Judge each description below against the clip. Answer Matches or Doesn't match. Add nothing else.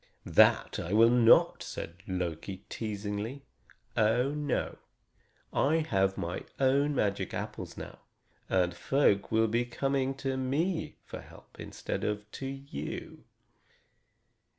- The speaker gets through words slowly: Matches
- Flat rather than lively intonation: Doesn't match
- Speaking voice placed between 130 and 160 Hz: Doesn't match